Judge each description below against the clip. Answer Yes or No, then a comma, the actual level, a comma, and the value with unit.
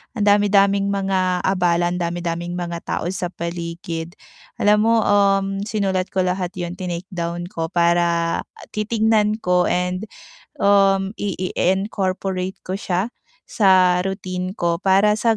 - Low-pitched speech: No, medium, 185 Hz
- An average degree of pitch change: No, narrow, 2.2 semitones